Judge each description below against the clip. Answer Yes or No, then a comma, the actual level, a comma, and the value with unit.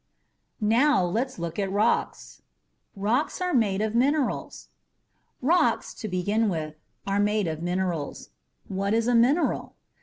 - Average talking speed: No, slow, 130 wpm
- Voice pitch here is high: Yes, high, 210 Hz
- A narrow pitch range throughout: No, average, 4.3 semitones